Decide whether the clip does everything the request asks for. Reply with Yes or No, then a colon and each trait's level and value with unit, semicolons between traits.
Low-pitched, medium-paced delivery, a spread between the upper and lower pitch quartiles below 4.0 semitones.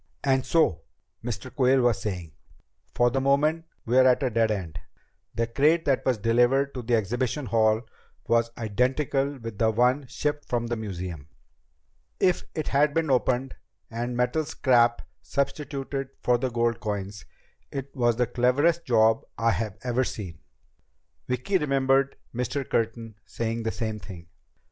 Yes: low, 120 Hz; average, 150 wpm; average, 3.3 semitones